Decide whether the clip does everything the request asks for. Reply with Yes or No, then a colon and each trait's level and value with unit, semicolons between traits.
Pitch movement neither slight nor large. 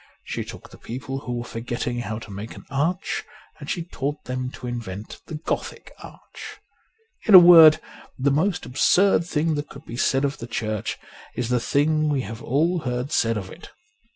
Yes: average, 4.5 semitones